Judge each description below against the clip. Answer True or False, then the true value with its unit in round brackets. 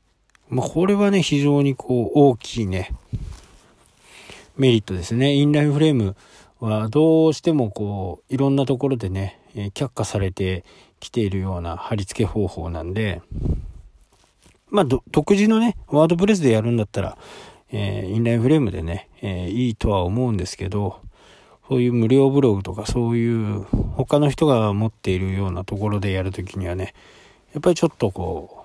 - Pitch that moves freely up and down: True (6.3 semitones)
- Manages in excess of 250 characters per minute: True (340 characters per minute)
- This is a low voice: True (115 Hz)